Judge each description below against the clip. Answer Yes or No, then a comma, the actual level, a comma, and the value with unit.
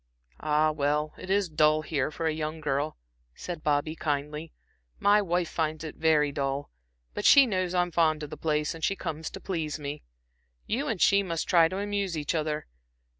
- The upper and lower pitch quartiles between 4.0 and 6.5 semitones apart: No, average, 2.8 semitones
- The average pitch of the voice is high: No, medium, 155 Hz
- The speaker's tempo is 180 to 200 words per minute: Yes, average, 195 wpm